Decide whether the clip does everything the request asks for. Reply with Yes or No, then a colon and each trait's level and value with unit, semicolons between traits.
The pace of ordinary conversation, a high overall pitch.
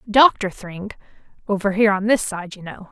Yes: average, 165 wpm; high, 200 Hz